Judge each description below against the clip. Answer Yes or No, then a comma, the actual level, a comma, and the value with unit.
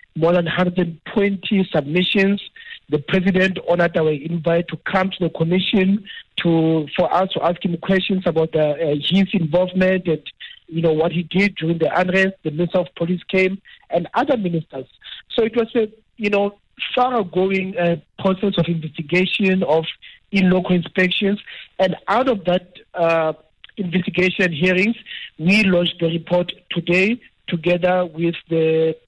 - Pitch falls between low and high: Yes, medium, 180 Hz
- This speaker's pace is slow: No, average, 155 wpm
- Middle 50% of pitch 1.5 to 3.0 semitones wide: Yes, narrow, 2.4 semitones